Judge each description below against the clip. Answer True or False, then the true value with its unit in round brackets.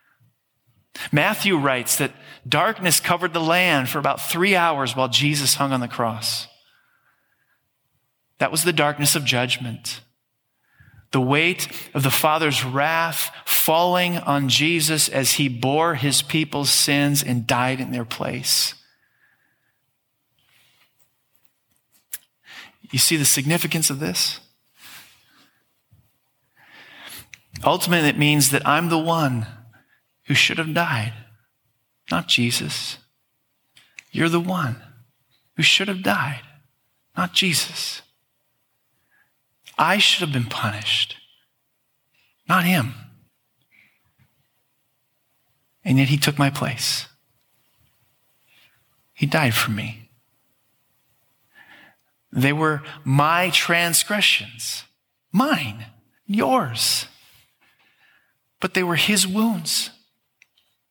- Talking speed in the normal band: False (100 wpm)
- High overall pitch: False (140 Hz)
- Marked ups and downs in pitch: False (4.9 semitones)